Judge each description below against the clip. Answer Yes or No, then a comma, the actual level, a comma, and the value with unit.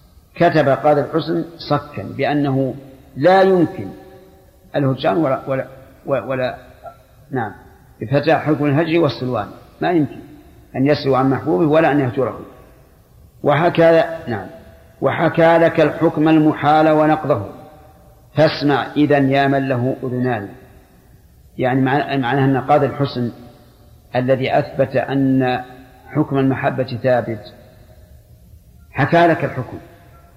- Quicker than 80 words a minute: Yes, average, 100 wpm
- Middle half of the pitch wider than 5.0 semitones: No, average, 3.2 semitones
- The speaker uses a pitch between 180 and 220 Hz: No, medium, 140 Hz